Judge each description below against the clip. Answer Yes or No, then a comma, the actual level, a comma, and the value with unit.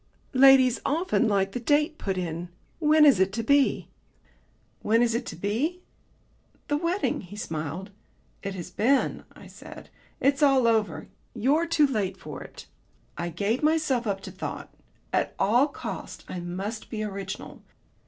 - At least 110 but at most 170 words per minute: Yes, average, 155 wpm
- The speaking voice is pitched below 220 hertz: No, high, 230 Hz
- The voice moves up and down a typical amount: No, wide, 6.6 semitones